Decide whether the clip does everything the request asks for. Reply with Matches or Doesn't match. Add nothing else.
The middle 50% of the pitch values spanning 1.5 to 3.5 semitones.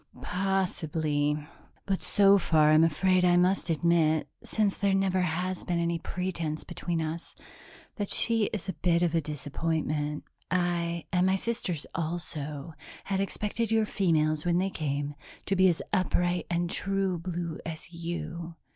Matches